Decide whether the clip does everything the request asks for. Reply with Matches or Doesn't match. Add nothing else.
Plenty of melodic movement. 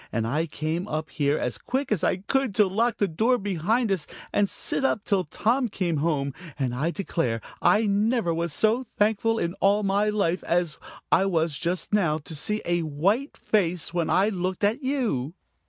Doesn't match